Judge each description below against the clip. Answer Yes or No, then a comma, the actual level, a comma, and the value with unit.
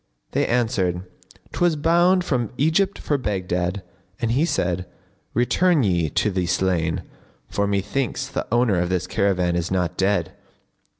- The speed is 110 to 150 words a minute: Yes, average, 140 wpm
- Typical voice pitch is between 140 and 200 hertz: No, low, 100 Hz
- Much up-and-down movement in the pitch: Yes, wide, 6.6 semitones